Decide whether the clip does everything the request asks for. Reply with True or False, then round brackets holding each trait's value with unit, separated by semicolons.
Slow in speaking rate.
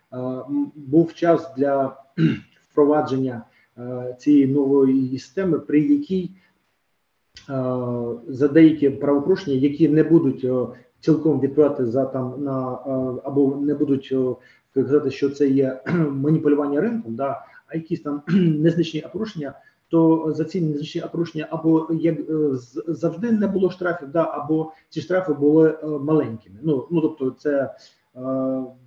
False (120 wpm)